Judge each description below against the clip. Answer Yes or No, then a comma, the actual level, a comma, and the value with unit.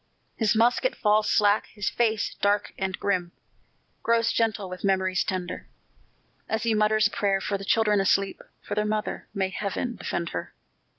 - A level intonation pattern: Yes, narrow, 2.1 semitones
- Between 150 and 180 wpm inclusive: Yes, average, 165 wpm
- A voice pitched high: Yes, high, 205 Hz